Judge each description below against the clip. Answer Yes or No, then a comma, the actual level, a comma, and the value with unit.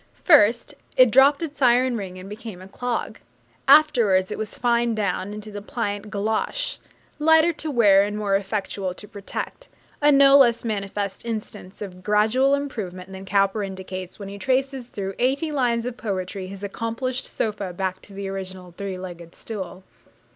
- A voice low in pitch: No, high, 210 Hz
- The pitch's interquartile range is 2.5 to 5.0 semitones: Yes, average, 4.4 semitones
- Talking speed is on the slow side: No, average, 165 wpm